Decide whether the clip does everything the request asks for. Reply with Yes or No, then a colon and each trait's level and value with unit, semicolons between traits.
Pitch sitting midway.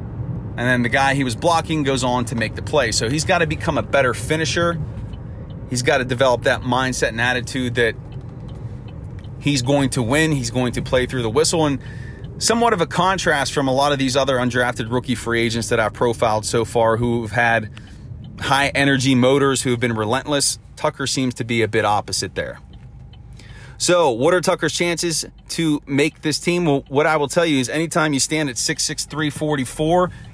No: low, 130 Hz